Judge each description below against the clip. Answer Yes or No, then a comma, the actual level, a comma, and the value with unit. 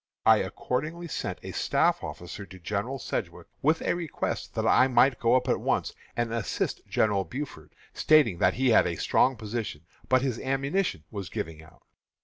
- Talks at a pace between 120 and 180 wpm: Yes, average, 175 wpm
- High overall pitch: No, low, 120 Hz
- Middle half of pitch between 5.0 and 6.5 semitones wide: Yes, wide, 5.5 semitones